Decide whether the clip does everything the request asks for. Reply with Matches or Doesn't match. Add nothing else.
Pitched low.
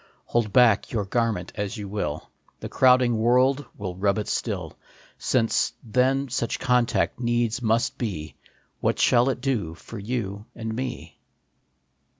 Matches